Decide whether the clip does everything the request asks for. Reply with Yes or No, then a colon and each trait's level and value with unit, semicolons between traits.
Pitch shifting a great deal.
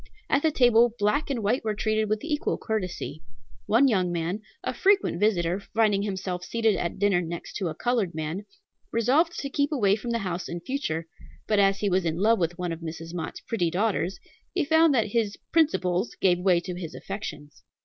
No: average, 4.8 semitones